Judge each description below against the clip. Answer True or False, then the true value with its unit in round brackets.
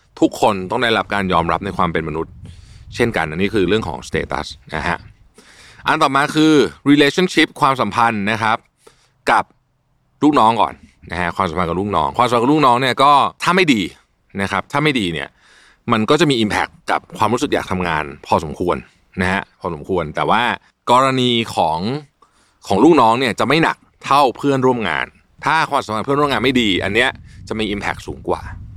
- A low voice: True (110 Hz)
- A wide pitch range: True (6.3 semitones)